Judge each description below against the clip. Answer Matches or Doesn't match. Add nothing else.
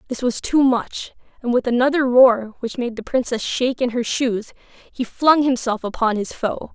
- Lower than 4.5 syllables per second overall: Doesn't match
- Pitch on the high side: Matches